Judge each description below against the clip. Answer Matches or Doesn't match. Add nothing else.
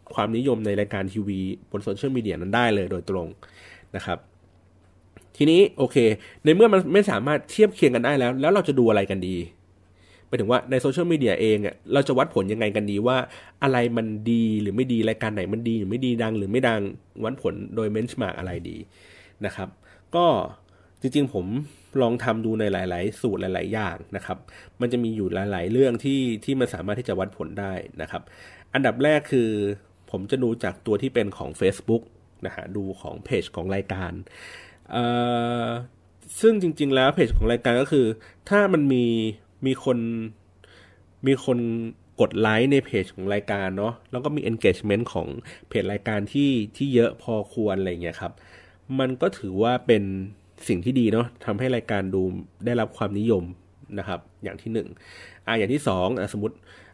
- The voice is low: Matches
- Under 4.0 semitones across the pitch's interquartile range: Doesn't match